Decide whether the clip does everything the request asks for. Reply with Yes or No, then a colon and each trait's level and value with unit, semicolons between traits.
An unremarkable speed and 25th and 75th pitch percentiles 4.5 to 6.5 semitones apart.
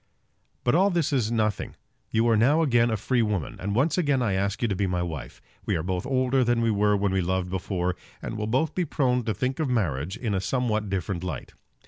No: fast, 235 wpm; average, 5.1 semitones